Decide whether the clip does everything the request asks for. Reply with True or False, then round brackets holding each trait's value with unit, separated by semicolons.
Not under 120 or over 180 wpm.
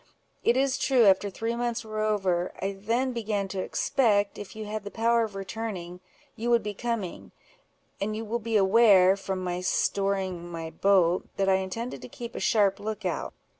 False (190 wpm)